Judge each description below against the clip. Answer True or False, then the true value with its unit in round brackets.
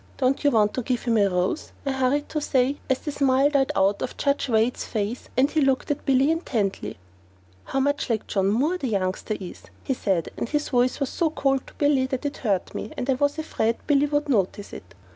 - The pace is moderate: False (220 wpm)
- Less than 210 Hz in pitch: False (260 Hz)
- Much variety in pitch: False (4.9 semitones)